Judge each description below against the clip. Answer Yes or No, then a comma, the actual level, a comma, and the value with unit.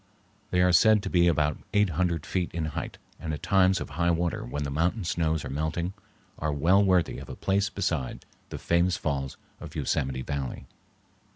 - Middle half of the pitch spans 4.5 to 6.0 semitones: No, average, 3.6 semitones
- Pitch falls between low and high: No, very low, 85 Hz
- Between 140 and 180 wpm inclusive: No, average, 190 wpm